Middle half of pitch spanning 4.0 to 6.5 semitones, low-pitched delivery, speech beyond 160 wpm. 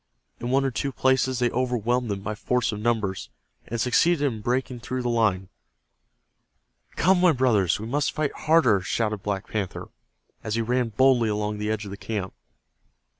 No: average, 3.4 semitones; low, 120 Hz; average, 175 wpm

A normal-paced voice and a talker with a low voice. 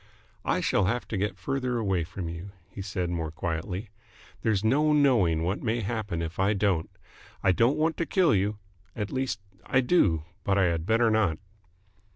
Yes: average, 185 wpm; low, 100 Hz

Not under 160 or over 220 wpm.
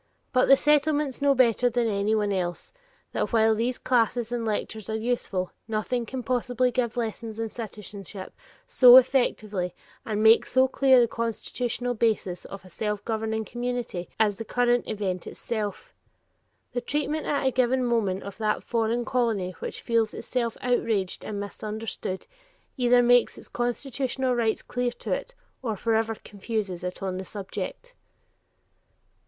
No: average, 150 wpm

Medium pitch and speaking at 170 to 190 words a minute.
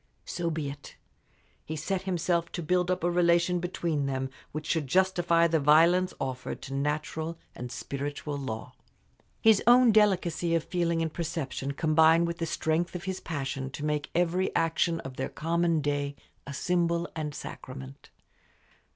No: medium, 165 Hz; average, 160 wpm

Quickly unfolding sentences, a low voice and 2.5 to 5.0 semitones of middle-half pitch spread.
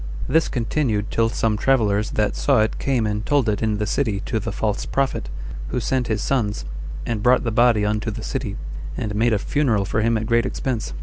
Yes: fast, 210 wpm; low, 110 Hz; average, 2.9 semitones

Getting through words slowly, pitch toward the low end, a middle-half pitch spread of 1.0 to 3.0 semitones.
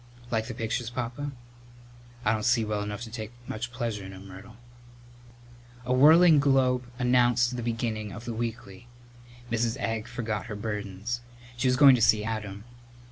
No: average, 165 wpm; low, 115 Hz; narrow, 2.5 semitones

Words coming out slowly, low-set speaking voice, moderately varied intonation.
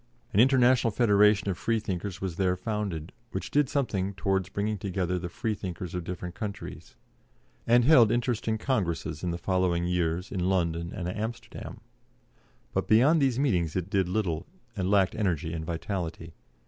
No: average, 155 wpm; very low, 95 Hz; average, 3.8 semitones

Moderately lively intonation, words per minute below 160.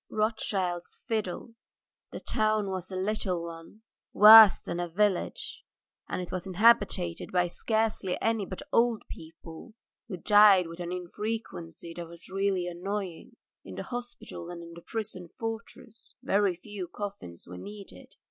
Yes: average, 3.6 semitones; average, 145 wpm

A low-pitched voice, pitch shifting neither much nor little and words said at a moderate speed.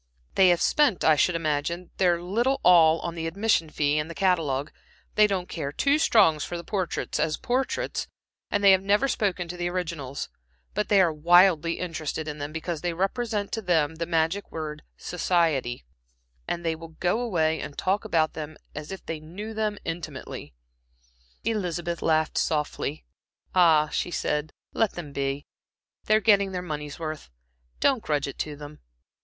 No: medium, 170 Hz; average, 3.8 semitones; average, 170 wpm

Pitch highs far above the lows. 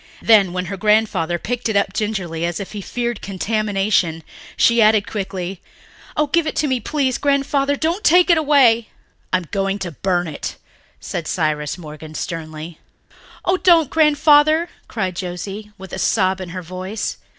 Yes: wide, 6.7 semitones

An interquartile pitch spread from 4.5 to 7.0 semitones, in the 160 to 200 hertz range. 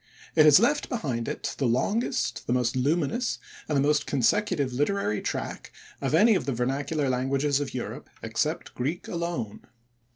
No: average, 5.0 semitones; medium, 145 Hz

